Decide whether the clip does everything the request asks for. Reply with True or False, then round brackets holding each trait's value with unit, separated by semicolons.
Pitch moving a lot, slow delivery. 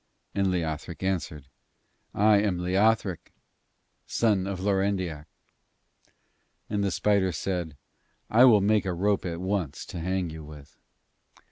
False (3.3 semitones; 125 wpm)